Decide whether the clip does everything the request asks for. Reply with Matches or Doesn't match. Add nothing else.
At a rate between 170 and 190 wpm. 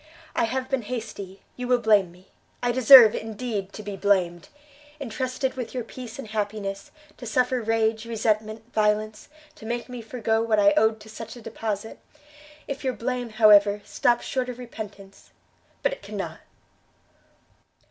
Doesn't match